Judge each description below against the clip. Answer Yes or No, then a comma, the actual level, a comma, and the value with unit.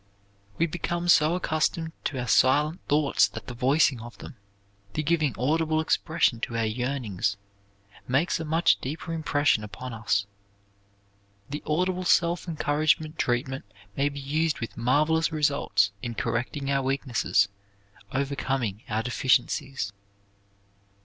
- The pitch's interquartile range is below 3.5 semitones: No, average, 4.4 semitones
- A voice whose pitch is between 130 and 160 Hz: Yes, medium, 140 Hz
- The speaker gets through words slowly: Yes, slow, 130 wpm